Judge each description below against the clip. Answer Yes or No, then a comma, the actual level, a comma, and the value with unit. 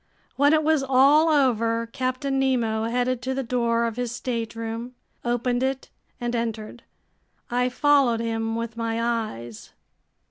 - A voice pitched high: Yes, high, 240 Hz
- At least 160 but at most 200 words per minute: No, average, 140 wpm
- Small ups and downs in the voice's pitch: Yes, narrow, 2.3 semitones